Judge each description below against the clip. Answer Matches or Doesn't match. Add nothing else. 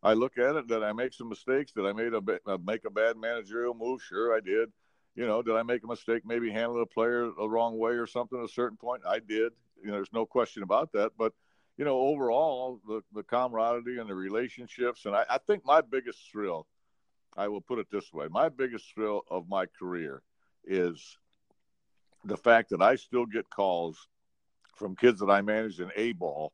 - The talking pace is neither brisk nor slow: Doesn't match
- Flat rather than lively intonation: Matches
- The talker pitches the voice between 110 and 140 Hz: Matches